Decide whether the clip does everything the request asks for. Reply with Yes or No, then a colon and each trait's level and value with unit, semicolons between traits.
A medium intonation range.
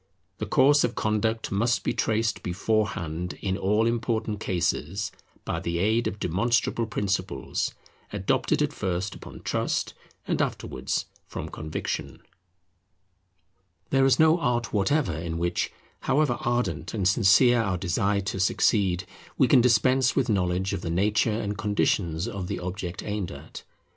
Yes: average, 4.5 semitones